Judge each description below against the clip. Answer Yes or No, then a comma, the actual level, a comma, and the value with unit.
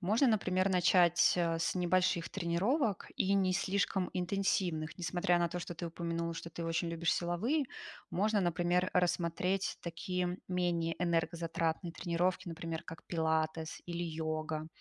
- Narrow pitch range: Yes, narrow, 1.9 semitones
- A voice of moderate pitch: Yes, medium, 175 Hz